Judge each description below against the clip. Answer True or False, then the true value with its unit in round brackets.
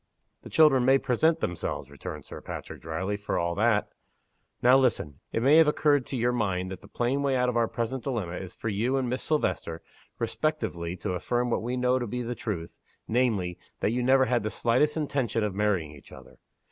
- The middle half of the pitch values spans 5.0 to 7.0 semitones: True (5.4 semitones)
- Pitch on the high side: False (120 Hz)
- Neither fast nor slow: False (210 wpm)